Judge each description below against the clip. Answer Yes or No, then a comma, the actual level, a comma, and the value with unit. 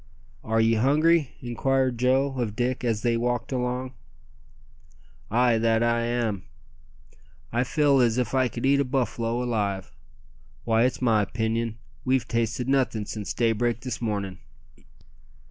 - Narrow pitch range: Yes, narrow, 2.2 semitones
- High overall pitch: No, low, 120 Hz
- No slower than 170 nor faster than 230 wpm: No, average, 140 wpm